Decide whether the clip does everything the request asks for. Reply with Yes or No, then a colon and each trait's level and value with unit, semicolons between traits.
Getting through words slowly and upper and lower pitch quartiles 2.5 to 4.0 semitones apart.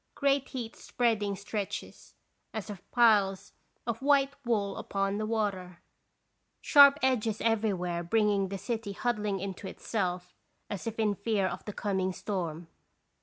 Yes: slow, 130 wpm; average, 2.9 semitones